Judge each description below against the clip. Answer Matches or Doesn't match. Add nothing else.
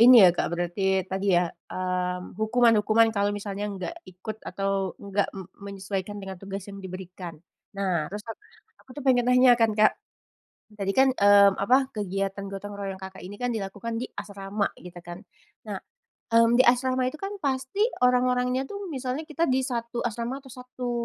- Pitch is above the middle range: Matches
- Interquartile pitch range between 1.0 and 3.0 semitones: Doesn't match